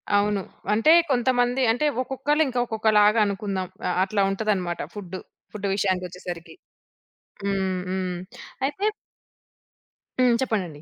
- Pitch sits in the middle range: No, high, 205 Hz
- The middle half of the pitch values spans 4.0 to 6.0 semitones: Yes, average, 4.5 semitones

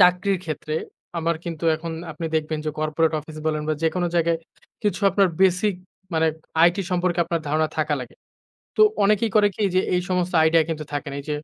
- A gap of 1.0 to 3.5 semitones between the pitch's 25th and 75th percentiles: Yes, average, 2.7 semitones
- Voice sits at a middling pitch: Yes, medium, 165 Hz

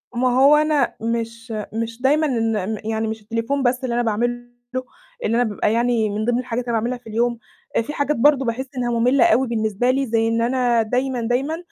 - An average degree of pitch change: No, narrow, 2.1 semitones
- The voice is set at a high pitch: Yes, high, 240 Hz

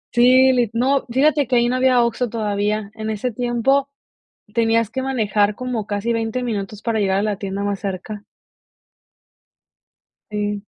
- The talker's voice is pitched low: No, high, 225 Hz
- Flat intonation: No, average, 3.3 semitones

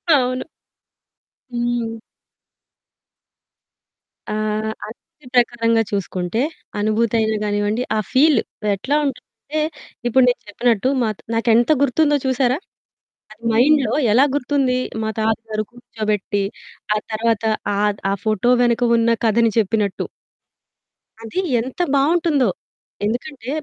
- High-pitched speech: Yes, high, 230 Hz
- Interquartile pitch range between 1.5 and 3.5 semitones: Yes, average, 3.1 semitones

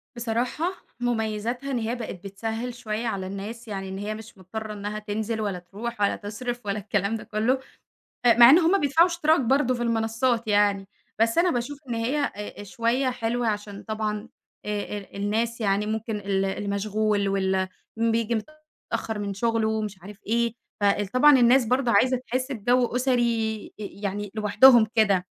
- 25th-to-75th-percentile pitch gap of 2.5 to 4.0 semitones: Yes, average, 2.8 semitones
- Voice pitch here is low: No, high, 220 Hz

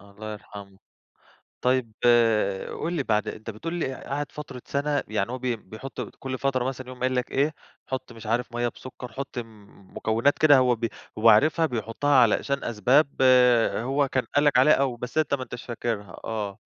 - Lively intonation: No, average, 3.6 semitones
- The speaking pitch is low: Yes, low, 125 Hz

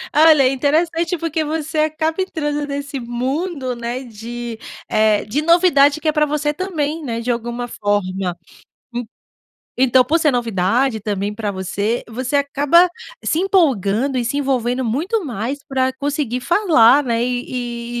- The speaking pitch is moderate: No, very high, 265 Hz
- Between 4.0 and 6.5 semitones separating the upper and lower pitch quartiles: Yes, average, 4.5 semitones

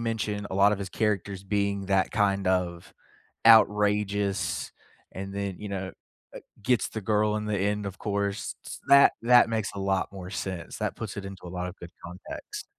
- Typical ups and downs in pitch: No, narrow, 1.5 semitones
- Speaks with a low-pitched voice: Yes, low, 100 Hz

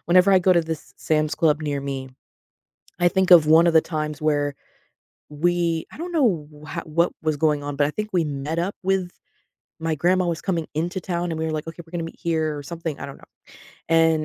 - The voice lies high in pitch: No, medium, 165 Hz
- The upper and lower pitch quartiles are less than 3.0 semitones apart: Yes, narrow, 2.4 semitones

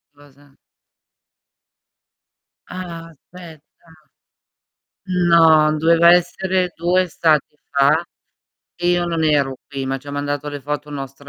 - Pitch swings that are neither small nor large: Yes, average, 3.2 semitones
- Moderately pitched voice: Yes, medium, 155 Hz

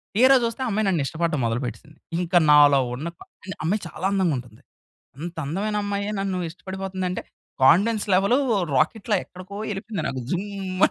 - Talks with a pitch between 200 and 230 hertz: No, medium, 185 Hz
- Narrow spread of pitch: No, average, 4.6 semitones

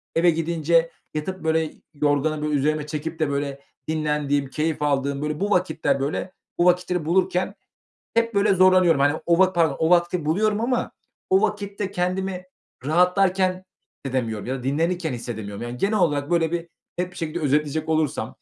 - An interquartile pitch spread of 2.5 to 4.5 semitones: Yes, average, 3.8 semitones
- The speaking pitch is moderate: Yes, medium, 160 Hz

